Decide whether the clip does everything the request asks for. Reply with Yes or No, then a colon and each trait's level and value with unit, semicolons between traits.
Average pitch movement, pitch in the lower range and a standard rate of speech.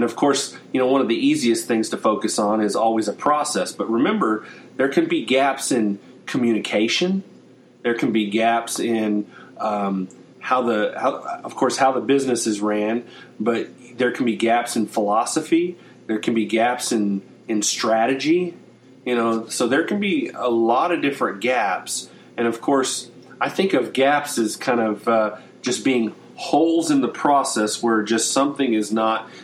Yes: average, 3.5 semitones; low, 115 Hz; average, 180 wpm